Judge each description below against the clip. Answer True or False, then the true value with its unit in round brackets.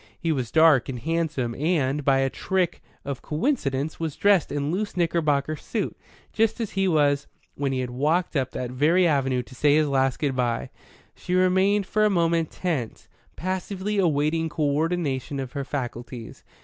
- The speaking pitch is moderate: True (150 Hz)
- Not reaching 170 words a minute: False (175 wpm)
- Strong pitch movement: False (4.6 semitones)